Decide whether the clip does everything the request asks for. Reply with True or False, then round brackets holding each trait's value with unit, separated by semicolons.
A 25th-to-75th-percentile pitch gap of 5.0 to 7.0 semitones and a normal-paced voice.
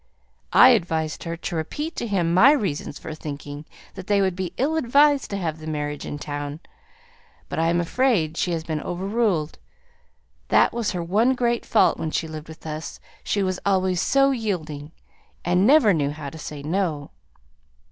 True (5.5 semitones; 180 wpm)